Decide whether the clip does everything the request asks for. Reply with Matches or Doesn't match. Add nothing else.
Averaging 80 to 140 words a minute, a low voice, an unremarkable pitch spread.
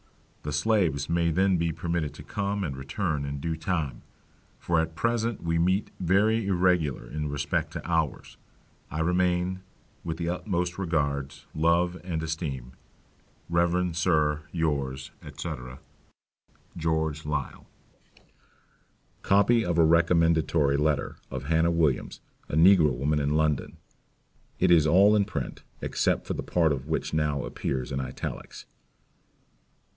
Matches